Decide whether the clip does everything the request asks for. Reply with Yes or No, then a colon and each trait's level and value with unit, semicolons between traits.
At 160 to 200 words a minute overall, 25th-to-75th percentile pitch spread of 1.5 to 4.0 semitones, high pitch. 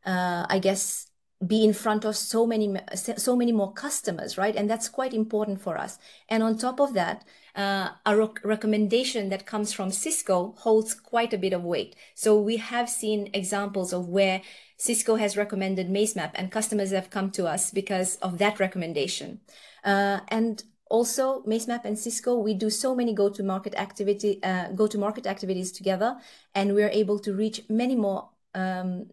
Yes: average, 185 wpm; narrow, 2.4 semitones; high, 210 Hz